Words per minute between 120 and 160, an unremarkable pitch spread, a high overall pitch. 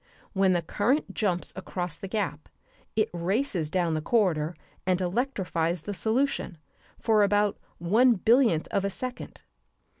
Yes: average, 140 wpm; average, 4.3 semitones; high, 195 Hz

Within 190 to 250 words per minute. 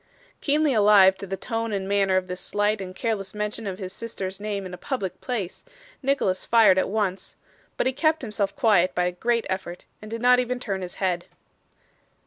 Yes: average, 200 wpm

